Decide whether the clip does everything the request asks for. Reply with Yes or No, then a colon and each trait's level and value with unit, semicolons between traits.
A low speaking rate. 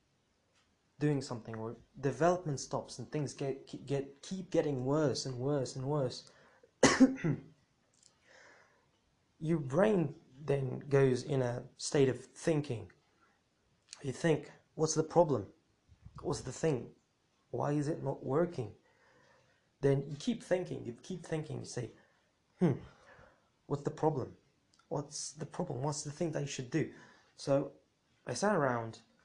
Yes: slow, 130 wpm